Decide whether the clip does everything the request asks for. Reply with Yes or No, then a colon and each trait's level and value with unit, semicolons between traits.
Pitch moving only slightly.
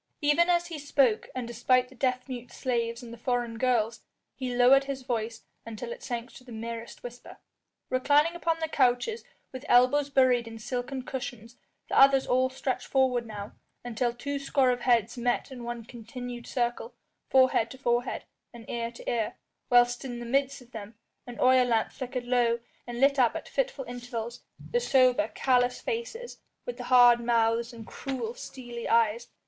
Yes: narrow, 2.0 semitones